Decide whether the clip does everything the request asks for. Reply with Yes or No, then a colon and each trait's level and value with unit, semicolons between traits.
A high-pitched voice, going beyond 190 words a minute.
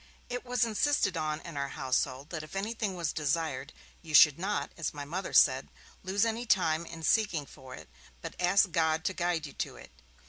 No: medium, 165 Hz; average, 200 wpm